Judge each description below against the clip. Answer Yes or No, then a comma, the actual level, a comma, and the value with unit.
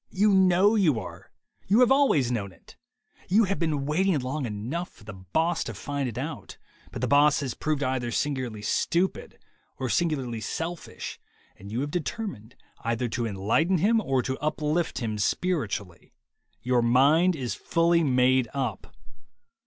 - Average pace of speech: Yes, average, 160 wpm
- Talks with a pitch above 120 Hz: Yes, medium, 140 Hz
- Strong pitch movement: Yes, wide, 6.2 semitones